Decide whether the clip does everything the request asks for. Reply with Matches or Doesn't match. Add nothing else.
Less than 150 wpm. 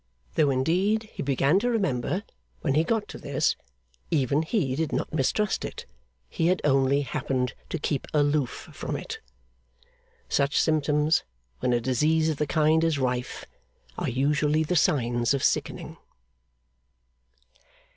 Matches